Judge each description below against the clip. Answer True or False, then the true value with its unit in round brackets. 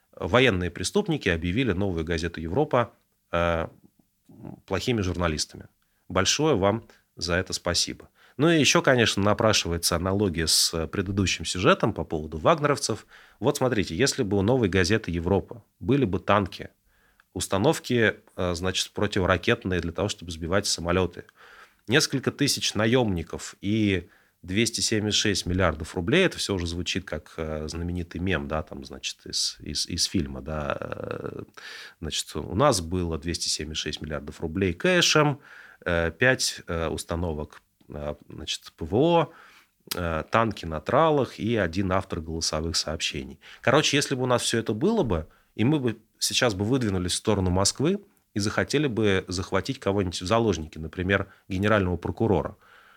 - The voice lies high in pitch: False (95 Hz)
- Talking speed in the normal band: True (130 wpm)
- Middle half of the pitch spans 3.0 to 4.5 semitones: False (5.1 semitones)